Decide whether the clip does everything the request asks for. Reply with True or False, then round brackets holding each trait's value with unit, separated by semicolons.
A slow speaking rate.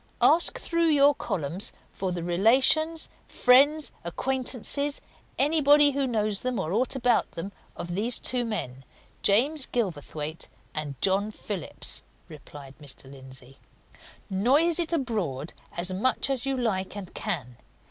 True (130 wpm)